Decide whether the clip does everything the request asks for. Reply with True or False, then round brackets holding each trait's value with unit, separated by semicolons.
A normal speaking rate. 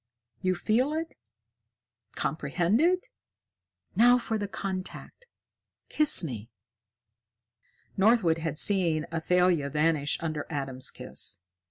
False (95 wpm)